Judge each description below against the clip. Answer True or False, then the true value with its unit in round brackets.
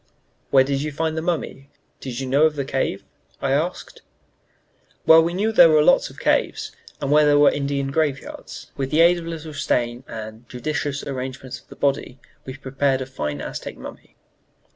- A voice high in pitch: False (140 Hz)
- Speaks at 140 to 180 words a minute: False (195 wpm)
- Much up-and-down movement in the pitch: False (2.8 semitones)